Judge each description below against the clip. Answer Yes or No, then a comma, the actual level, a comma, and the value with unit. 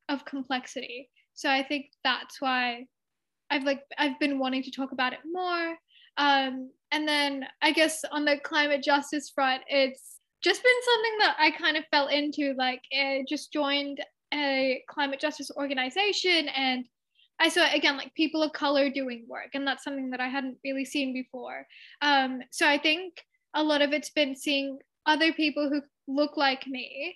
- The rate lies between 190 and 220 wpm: No, average, 175 wpm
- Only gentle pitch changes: Yes, narrow, 2.2 semitones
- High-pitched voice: Yes, very high, 285 Hz